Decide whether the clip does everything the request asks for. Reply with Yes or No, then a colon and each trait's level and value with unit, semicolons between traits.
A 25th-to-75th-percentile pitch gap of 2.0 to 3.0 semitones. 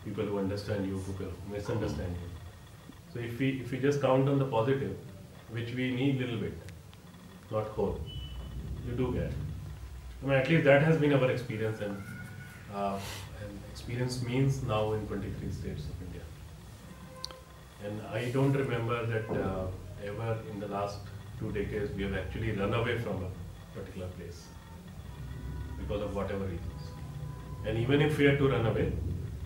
No: average, 4.7 semitones